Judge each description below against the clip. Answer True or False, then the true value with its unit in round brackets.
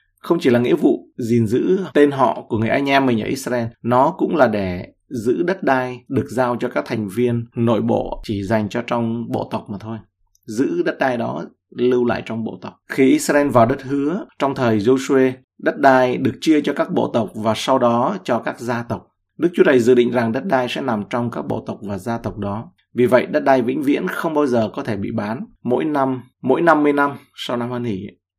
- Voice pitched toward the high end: False (125 Hz)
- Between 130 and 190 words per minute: False (235 wpm)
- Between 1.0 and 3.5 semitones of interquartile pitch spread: True (2.9 semitones)